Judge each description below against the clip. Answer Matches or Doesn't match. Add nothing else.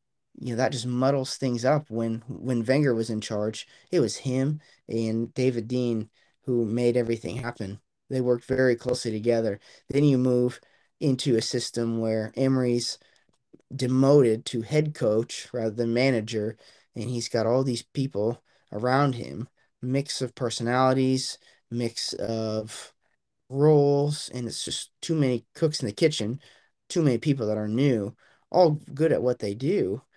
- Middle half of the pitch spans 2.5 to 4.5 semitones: Matches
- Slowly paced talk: Doesn't match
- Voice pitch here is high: Doesn't match